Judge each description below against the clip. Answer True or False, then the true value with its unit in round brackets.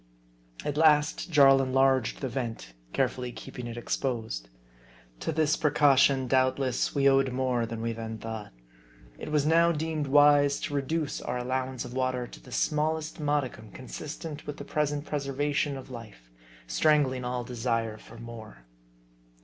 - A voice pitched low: True (130 Hz)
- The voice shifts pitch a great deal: False (3.6 semitones)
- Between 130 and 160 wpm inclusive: True (155 wpm)